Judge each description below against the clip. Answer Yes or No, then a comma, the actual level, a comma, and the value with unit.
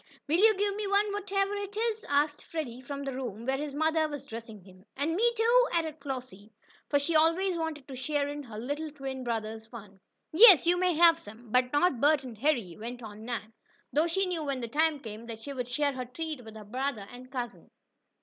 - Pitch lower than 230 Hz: No, very high, 285 Hz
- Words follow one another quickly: Yes, fast, 220 wpm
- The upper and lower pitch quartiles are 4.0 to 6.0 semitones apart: Yes, wide, 5.5 semitones